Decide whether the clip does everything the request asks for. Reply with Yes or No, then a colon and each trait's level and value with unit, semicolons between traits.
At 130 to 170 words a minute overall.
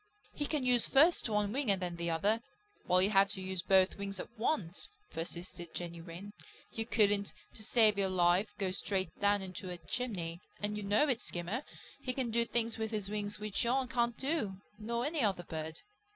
No: average, 200 wpm